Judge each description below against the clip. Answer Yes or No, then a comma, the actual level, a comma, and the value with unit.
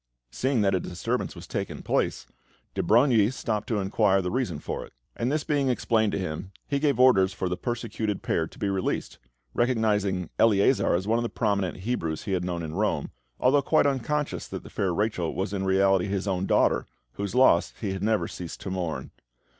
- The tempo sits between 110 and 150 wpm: No, average, 200 wpm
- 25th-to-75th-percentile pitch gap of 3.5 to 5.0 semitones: Yes, average, 4.1 semitones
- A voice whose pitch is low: Yes, low, 100 Hz